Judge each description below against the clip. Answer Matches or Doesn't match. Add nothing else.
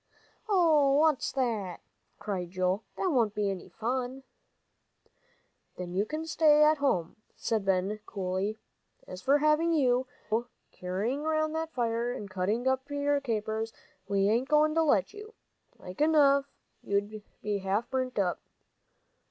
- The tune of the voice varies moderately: Doesn't match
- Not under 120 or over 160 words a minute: Matches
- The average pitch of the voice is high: Matches